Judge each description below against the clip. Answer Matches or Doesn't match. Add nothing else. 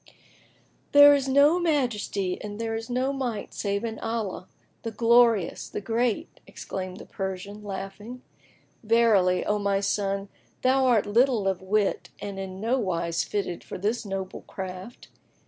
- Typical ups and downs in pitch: Matches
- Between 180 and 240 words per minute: Doesn't match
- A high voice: Matches